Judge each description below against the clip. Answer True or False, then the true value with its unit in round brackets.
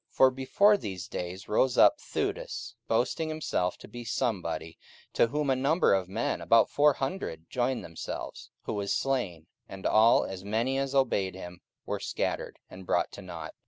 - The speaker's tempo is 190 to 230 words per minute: False (175 wpm)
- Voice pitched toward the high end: False (115 Hz)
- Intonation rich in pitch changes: True (6.6 semitones)